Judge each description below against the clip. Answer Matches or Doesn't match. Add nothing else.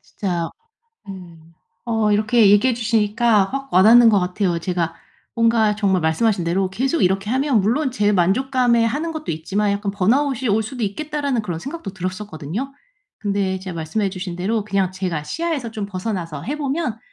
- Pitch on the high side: Matches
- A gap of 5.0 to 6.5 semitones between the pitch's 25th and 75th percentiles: Doesn't match